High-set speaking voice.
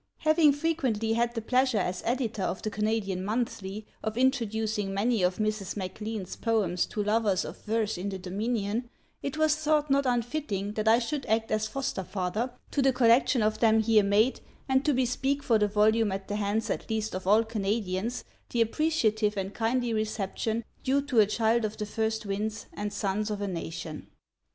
Yes: high, 220 Hz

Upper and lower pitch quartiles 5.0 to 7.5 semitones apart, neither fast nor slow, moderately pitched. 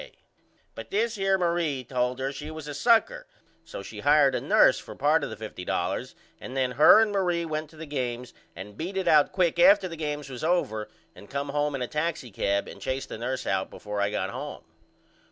No: wide, 5.5 semitones; fast, 215 wpm; medium, 150 Hz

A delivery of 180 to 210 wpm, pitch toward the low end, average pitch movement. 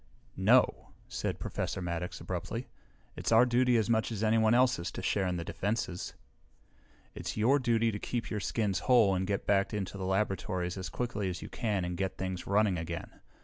Yes: average, 190 wpm; low, 100 Hz; average, 3.5 semitones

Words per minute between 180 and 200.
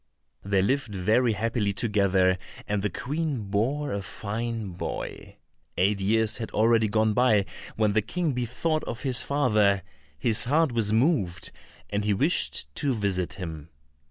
No: average, 155 wpm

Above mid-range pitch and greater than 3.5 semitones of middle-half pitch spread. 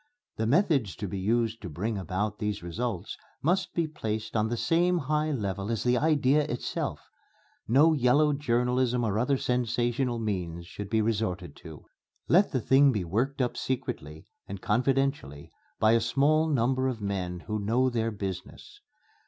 No: low, 115 Hz; average, 4.8 semitones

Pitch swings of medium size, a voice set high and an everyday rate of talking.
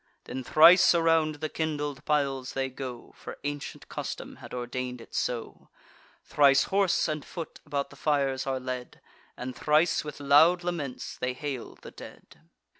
No: average, 3.1 semitones; medium, 145 Hz; average, 155 wpm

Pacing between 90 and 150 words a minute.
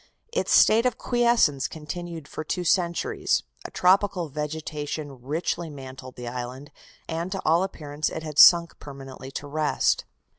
Yes: average, 145 wpm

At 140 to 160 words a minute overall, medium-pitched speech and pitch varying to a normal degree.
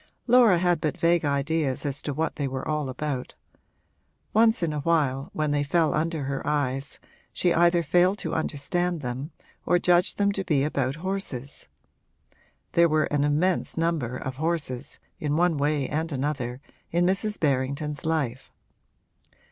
Yes: average, 155 wpm; medium, 150 Hz; average, 3.6 semitones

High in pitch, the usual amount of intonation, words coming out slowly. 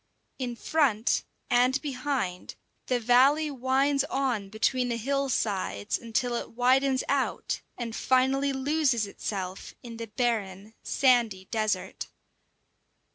Yes: high, 245 Hz; average, 3.5 semitones; slow, 115 wpm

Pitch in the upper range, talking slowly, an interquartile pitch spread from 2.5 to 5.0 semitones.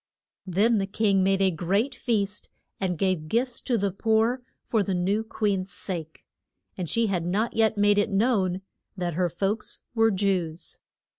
No: high, 195 Hz; average, 165 wpm; average, 3.1 semitones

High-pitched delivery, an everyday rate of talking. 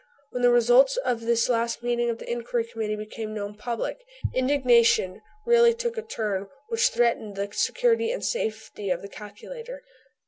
Yes: high, 235 Hz; average, 165 wpm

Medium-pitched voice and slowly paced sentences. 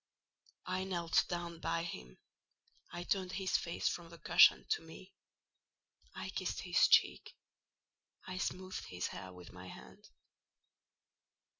Yes: medium, 170 Hz; slow, 130 wpm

